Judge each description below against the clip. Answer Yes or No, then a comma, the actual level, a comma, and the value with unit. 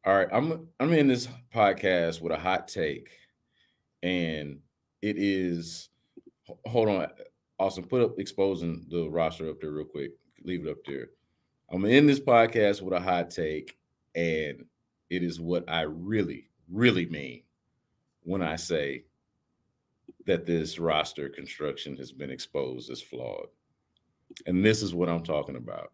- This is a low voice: Yes, very low, 90 Hz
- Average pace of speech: Yes, average, 150 wpm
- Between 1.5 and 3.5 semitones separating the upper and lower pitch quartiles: No, average, 4.2 semitones